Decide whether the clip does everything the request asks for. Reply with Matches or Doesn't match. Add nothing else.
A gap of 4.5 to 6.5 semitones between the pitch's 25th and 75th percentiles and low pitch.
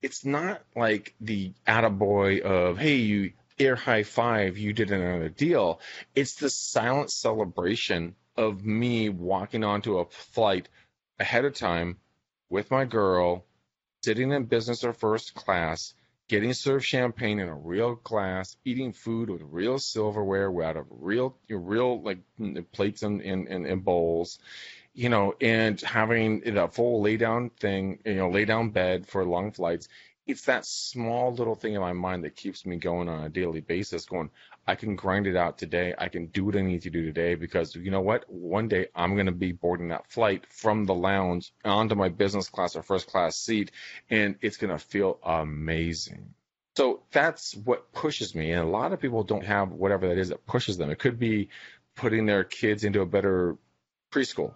Doesn't match